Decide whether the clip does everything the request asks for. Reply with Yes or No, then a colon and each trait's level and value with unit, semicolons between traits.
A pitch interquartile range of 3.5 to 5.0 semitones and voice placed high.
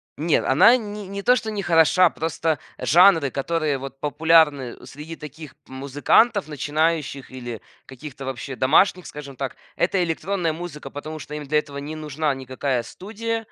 No: average, 3.9 semitones; medium, 155 Hz